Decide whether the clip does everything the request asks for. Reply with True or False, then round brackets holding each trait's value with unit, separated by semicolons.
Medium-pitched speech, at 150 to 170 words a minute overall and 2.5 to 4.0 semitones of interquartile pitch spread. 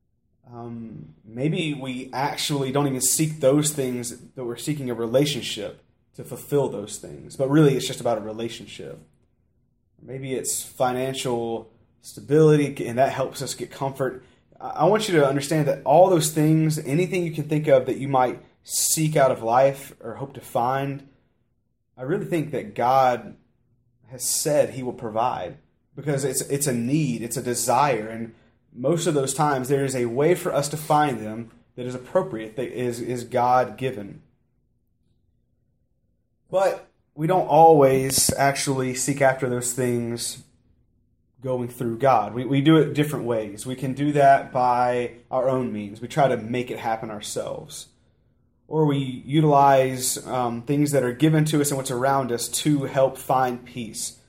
False (130 Hz; 165 wpm; 3.1 semitones)